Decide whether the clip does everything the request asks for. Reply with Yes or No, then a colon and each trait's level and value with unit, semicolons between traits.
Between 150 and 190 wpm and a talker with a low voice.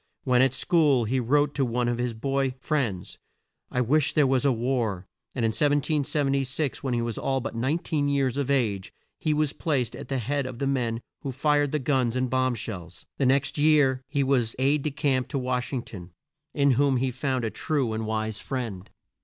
No: fast, 205 wpm; low, 130 Hz